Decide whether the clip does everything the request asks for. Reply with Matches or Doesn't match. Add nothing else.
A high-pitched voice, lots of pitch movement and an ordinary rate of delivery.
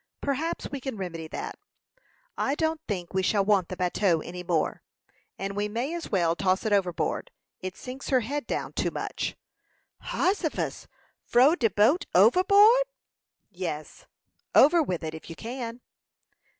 Matches